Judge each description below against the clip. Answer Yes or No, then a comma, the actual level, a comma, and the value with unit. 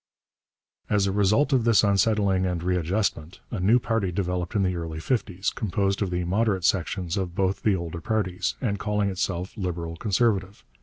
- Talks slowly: No, average, 170 wpm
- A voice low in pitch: Yes, very low, 95 Hz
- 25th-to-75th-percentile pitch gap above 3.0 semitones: No, average, 2.7 semitones